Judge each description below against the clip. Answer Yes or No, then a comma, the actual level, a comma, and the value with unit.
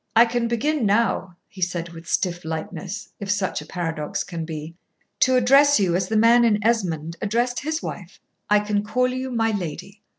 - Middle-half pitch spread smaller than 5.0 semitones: No, average, 5.3 semitones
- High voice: Yes, high, 205 Hz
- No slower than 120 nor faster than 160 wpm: No, average, 190 wpm